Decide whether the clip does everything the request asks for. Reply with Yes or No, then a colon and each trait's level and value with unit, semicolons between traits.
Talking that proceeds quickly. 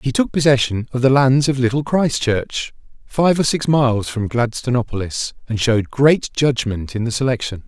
No: average, 170 wpm